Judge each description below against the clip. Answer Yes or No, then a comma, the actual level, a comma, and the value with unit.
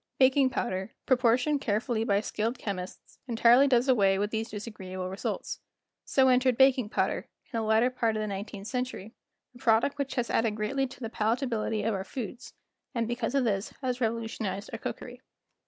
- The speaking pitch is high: Yes, high, 230 Hz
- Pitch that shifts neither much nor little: Yes, average, 3.1 semitones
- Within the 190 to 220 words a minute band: No, average, 175 wpm